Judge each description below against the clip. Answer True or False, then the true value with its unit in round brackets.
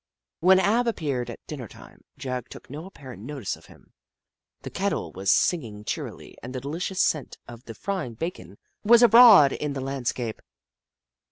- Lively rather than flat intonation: True (7.2 semitones)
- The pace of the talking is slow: False (170 wpm)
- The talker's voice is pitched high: False (140 Hz)